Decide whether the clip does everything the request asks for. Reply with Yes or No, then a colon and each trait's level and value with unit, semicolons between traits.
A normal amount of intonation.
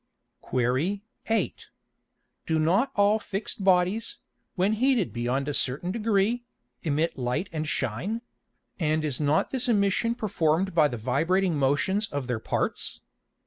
No: wide, 6.2 semitones